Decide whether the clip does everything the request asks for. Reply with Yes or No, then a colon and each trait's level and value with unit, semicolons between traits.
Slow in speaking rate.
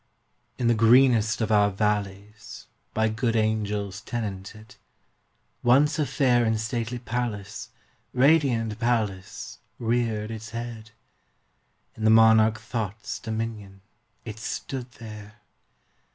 Yes: slow, 110 wpm